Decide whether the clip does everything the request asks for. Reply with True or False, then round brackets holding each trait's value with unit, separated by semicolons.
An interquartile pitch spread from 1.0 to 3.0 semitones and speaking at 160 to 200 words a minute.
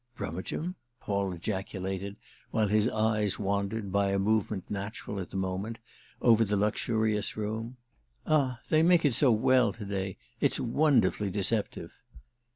False (2.5 semitones; 135 wpm)